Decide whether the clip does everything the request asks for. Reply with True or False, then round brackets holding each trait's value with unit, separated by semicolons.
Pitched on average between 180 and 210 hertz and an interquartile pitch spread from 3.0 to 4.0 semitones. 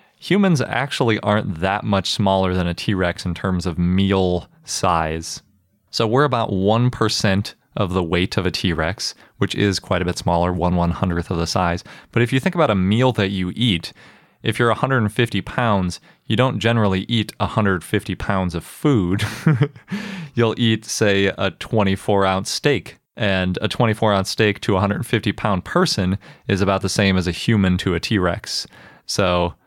False (100 Hz; 3.7 semitones)